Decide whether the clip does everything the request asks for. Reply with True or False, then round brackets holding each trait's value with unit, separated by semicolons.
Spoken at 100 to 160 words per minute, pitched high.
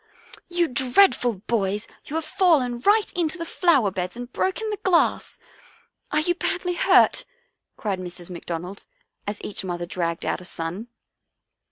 True (155 wpm; 245 Hz)